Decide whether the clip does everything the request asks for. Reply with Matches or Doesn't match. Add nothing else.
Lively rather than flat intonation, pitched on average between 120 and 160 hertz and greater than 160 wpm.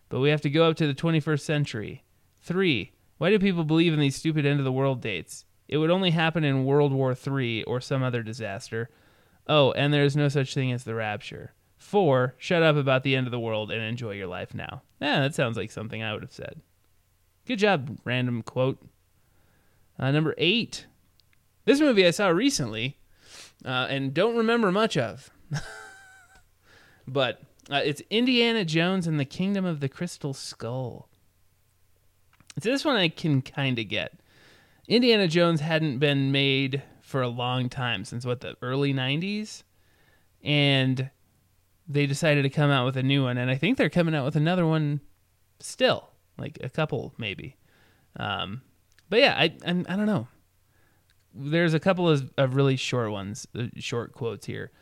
Matches